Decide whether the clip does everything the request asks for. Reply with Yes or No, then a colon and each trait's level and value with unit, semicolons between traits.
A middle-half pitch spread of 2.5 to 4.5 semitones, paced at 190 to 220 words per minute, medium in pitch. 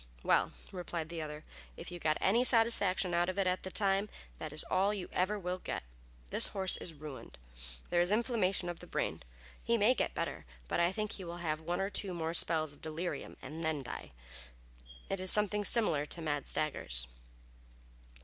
Yes: average, 3.8 semitones; average, 195 wpm; medium, 175 Hz